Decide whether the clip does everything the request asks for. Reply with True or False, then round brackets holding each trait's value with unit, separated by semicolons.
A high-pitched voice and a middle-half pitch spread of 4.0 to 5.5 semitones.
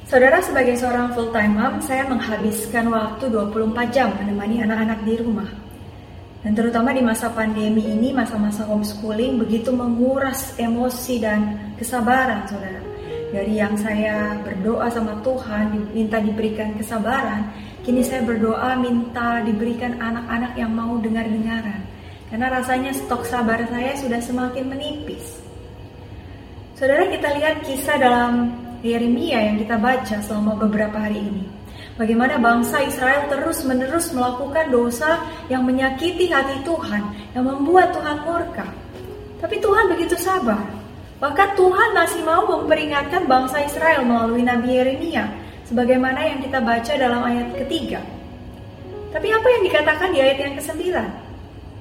False (245 Hz; 3.6 semitones)